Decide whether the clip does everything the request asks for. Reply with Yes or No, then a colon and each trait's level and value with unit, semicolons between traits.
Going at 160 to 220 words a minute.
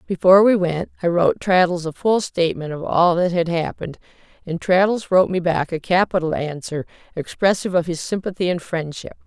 Yes: average, 180 wpm